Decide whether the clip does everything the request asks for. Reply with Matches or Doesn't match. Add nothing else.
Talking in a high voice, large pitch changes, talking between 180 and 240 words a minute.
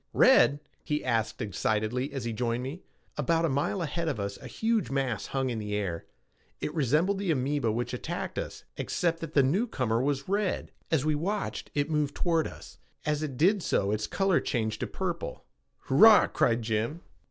Doesn't match